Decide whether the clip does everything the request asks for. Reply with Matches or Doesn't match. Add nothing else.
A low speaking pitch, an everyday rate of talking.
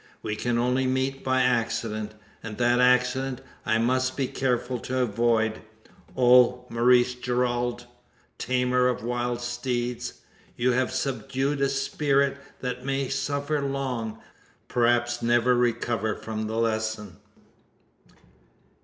Doesn't match